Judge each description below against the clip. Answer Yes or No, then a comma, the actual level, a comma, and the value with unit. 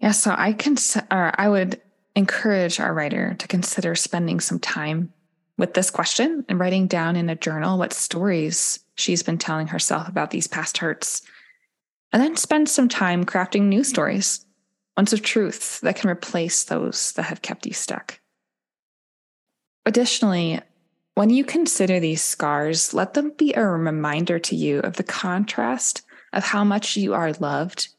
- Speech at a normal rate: Yes, average, 165 wpm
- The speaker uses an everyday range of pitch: Yes, average, 4.1 semitones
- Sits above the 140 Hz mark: Yes, medium, 185 Hz